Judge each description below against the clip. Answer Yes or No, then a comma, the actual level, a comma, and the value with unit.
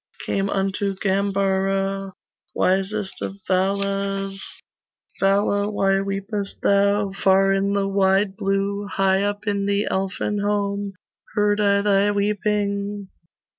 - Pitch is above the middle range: Yes, high, 200 Hz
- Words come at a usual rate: No, slow, 110 wpm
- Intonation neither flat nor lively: No, narrow, 0.8 semitones